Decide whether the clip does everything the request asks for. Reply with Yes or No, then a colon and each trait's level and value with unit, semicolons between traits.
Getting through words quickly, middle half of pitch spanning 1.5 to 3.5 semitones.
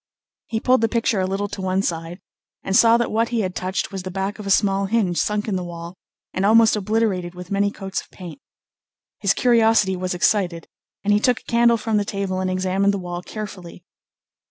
Yes: fast, 215 wpm; average, 2.8 semitones